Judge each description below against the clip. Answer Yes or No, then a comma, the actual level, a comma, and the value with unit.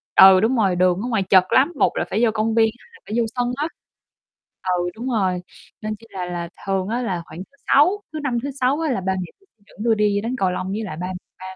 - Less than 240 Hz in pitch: Yes, high, 215 Hz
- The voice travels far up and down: No, average, 4.7 semitones